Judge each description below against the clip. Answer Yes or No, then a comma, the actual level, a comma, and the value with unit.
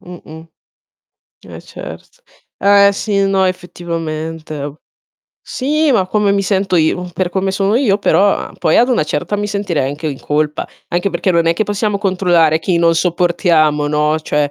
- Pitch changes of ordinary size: Yes, average, 4.0 semitones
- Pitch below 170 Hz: No, medium, 180 Hz